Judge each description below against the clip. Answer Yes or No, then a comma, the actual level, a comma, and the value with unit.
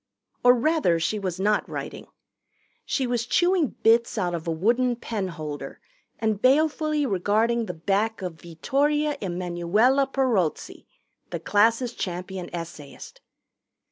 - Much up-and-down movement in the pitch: Yes, wide, 6.3 semitones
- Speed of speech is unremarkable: No, slow, 125 wpm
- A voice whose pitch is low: No, high, 215 Hz